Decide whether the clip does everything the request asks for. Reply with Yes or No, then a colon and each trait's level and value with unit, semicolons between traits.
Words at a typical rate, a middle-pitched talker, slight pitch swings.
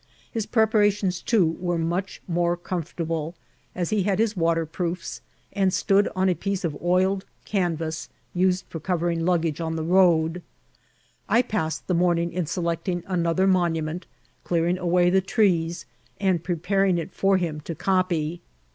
Yes: average, 150 wpm; medium, 175 Hz; narrow, 2.3 semitones